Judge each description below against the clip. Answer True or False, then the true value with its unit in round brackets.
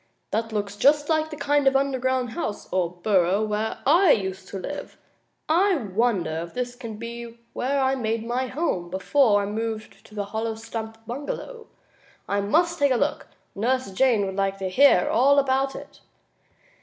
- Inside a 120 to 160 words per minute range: False (180 wpm)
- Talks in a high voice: True (230 Hz)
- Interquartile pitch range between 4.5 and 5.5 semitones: True (5.1 semitones)